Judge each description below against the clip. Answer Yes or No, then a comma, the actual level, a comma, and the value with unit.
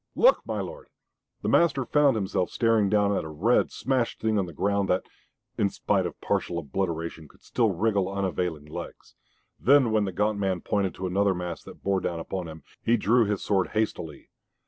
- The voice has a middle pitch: No, low, 100 Hz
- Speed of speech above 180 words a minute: Yes, average, 190 wpm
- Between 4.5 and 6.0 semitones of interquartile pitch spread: No, average, 3.7 semitones